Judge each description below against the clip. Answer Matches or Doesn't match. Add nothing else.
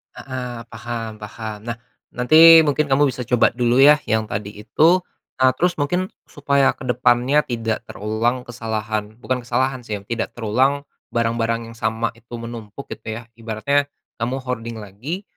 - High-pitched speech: Doesn't match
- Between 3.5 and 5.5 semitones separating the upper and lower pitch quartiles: Doesn't match